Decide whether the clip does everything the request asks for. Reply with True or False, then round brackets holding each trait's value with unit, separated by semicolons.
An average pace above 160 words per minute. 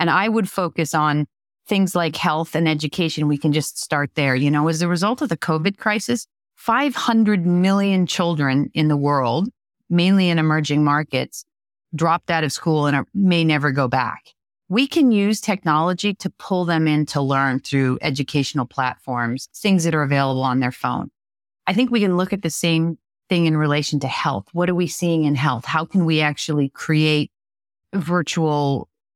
True (185 wpm)